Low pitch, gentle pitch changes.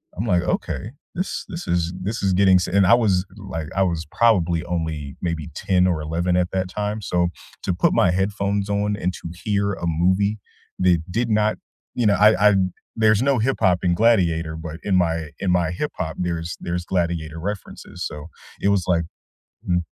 No: very low, 90 Hz; average, 3.1 semitones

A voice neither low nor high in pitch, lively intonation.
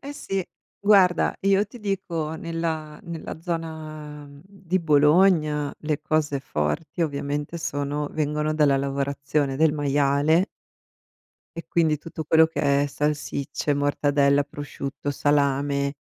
No: medium, 150 Hz; narrow, 2.5 semitones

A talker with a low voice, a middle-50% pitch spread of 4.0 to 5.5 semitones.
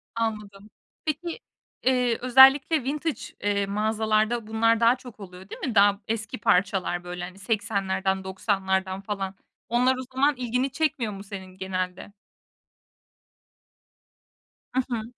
No: high, 215 Hz; average, 4.3 semitones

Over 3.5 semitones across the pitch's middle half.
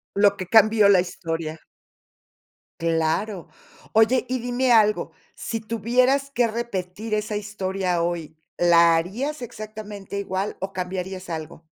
Yes: average, 3.9 semitones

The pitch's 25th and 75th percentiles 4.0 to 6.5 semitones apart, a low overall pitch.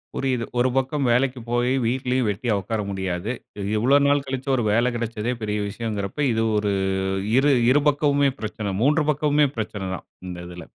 Yes: average, 4.3 semitones; low, 120 Hz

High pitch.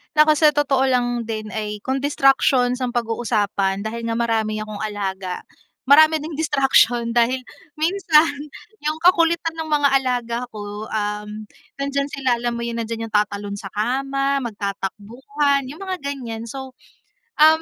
Yes: high, 245 Hz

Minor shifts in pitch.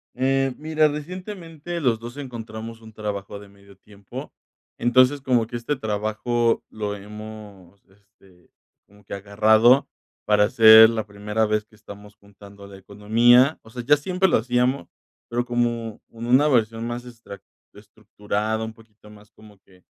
No: average, 3.0 semitones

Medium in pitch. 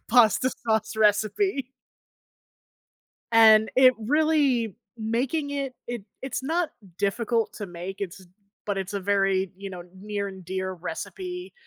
No: high, 220 Hz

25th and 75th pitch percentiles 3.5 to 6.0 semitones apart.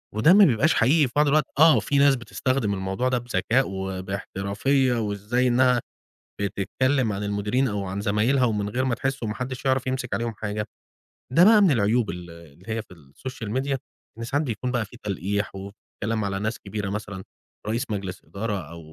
Yes: average, 4.5 semitones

